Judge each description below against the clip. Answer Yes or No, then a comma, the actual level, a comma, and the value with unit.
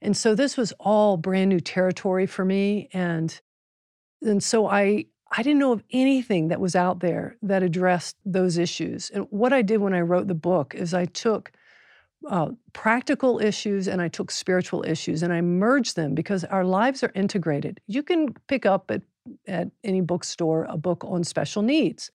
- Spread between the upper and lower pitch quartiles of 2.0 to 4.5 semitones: Yes, average, 3.8 semitones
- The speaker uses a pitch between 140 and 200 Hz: Yes, high, 190 Hz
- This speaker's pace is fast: No, average, 185 wpm